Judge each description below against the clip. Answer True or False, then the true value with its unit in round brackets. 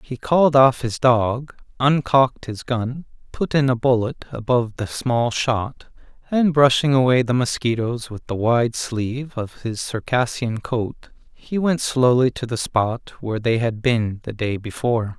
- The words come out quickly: False (165 wpm)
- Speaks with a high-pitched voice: False (120 Hz)